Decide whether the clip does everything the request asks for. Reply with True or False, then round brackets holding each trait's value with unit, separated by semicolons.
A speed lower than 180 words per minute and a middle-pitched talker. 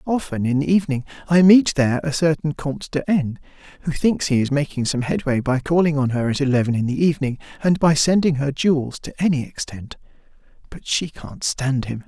False (205 wpm; 145 Hz)